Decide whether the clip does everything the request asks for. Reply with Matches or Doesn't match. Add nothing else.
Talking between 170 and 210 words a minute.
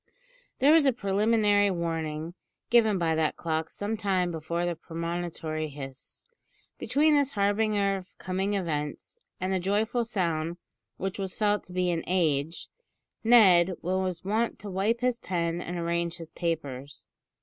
Doesn't match